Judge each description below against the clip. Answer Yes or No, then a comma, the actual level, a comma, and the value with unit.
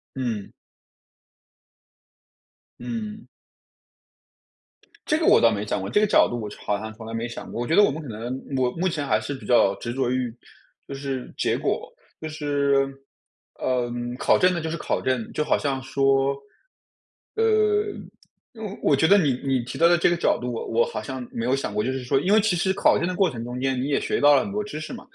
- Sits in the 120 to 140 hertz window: Yes, low, 135 Hz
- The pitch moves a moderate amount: No, wide, 5.9 semitones